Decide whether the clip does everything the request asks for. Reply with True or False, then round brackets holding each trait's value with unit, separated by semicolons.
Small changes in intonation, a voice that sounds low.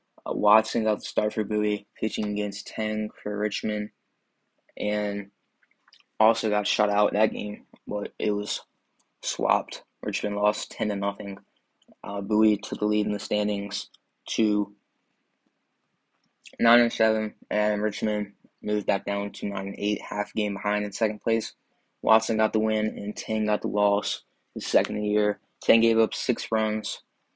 True (0.8 semitones; 105 Hz)